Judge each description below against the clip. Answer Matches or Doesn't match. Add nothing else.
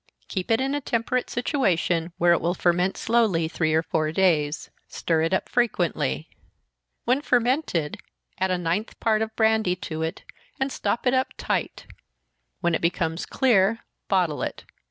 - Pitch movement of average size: Doesn't match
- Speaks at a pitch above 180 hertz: Matches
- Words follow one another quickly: Doesn't match